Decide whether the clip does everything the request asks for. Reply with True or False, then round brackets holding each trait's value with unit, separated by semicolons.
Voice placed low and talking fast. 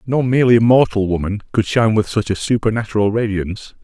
False (110 Hz; 170 wpm)